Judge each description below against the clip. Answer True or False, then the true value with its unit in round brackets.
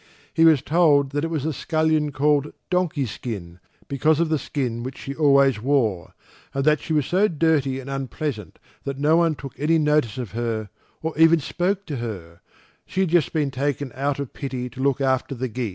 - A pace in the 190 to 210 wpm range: True (200 wpm)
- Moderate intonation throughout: True (3.6 semitones)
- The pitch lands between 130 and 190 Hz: True (140 Hz)